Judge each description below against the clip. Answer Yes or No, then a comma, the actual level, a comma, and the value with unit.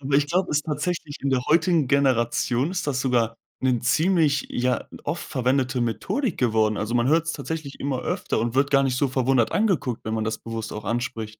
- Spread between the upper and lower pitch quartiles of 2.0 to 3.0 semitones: No, average, 4.0 semitones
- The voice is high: No, low, 130 Hz